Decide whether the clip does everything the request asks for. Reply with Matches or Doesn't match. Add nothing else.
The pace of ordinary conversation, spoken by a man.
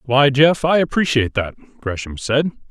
Matches